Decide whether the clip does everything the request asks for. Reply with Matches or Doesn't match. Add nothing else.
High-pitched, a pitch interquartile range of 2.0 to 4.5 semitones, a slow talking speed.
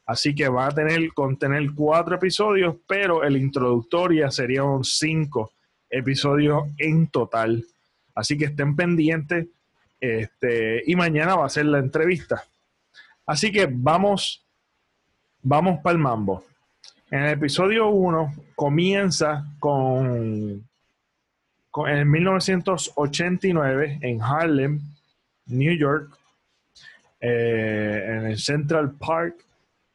Doesn't match